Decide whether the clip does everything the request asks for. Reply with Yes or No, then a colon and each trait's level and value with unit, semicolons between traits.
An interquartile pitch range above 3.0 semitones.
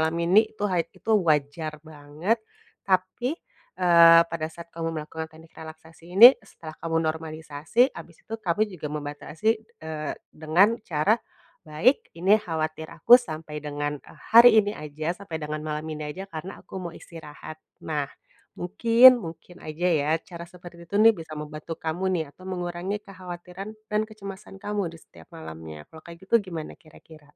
Yes: average, 3.6 semitones